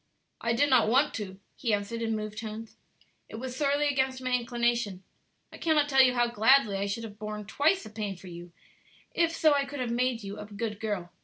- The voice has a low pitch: No, high, 230 Hz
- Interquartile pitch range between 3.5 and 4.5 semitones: Yes, average, 3.9 semitones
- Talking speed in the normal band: No, fast, 220 wpm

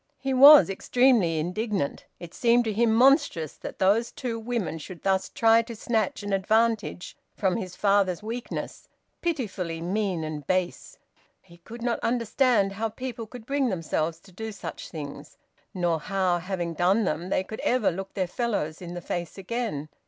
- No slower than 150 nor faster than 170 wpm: Yes, average, 165 wpm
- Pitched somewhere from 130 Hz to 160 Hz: No, high, 200 Hz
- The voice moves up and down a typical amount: Yes, average, 4.8 semitones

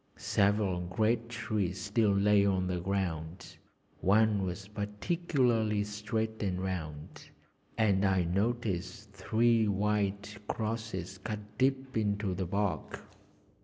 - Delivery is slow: Yes, slow, 110 wpm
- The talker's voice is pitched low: Yes, low, 100 Hz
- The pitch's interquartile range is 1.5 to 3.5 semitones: Yes, narrow, 2.6 semitones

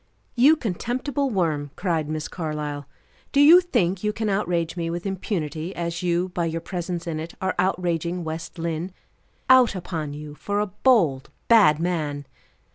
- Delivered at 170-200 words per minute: No, average, 160 wpm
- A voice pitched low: No, medium, 175 Hz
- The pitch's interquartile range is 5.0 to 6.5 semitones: No, average, 3.9 semitones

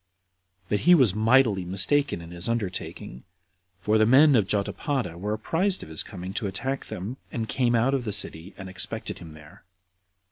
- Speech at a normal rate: Yes, average, 180 wpm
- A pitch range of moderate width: No, wide, 5.8 semitones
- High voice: No, low, 105 Hz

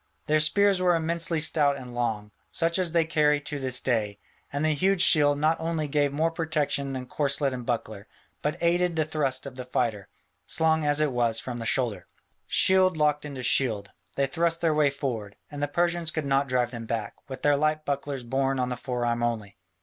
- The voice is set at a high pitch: No, medium, 145 Hz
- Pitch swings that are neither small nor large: Yes, average, 4.3 semitones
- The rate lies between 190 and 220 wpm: Yes, fast, 205 wpm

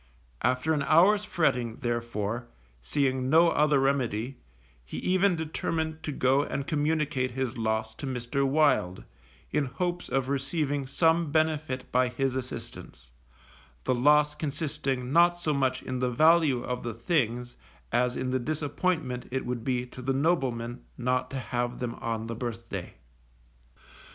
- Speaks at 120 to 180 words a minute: Yes, average, 145 wpm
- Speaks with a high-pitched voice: No, low, 130 Hz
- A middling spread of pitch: Yes, average, 3.9 semitones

